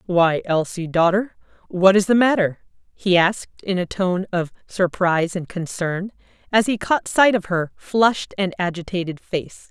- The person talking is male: No, female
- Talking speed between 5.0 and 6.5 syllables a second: No, 4.5 syllables/s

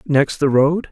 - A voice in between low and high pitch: Yes, medium, 145 Hz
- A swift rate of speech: No, average, 195 wpm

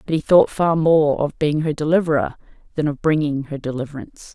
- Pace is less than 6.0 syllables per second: Yes, 5.7 syllables/s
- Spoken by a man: No, female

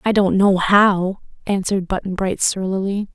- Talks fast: No, average, 155 wpm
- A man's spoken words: No, female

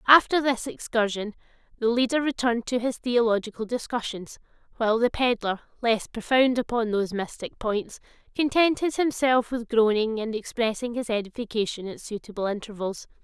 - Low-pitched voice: No, high, 230 Hz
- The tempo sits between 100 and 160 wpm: Yes, slow, 135 wpm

